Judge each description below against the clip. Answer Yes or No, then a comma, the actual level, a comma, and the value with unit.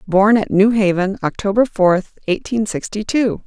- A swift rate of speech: No, average, 155 wpm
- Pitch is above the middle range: Yes, high, 205 Hz